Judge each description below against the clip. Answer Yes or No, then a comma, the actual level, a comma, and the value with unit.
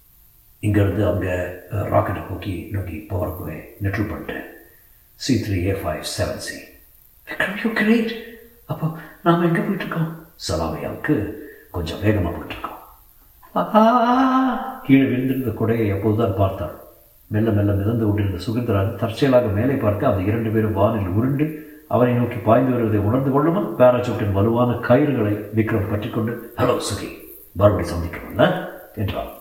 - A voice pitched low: Yes, low, 110 Hz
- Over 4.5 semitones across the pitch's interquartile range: Yes, wide, 5.4 semitones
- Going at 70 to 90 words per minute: No, average, 120 wpm